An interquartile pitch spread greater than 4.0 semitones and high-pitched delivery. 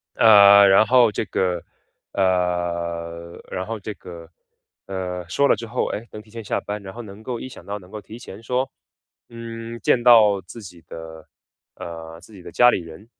No: average, 4.5 semitones; low, 100 Hz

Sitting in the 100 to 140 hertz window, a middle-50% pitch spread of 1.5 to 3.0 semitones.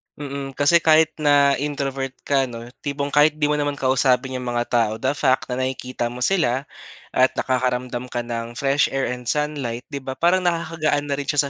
Yes: low, 135 Hz; average, 2.7 semitones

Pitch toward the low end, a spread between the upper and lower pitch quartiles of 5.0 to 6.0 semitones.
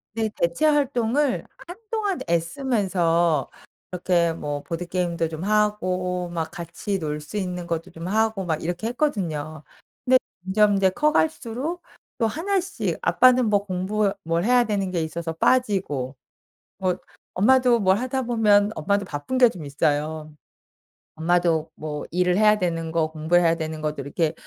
No: medium, 185 Hz; average, 5.3 semitones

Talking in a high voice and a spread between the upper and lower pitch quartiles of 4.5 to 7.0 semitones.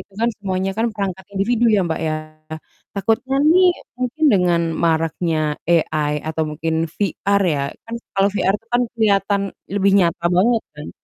Yes: high, 195 Hz; average, 4.8 semitones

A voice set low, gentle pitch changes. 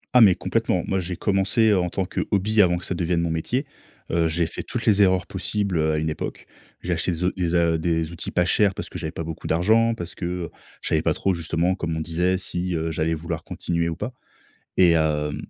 Yes: very low, 85 Hz; narrow, 2.3 semitones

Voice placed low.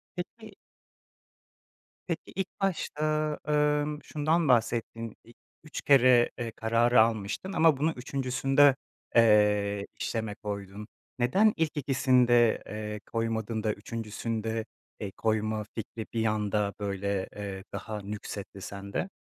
Yes: low, 115 Hz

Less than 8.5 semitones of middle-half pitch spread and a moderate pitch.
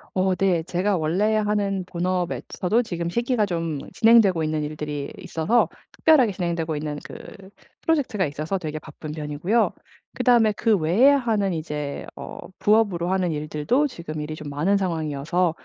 Yes: average, 5.3 semitones; medium, 180 Hz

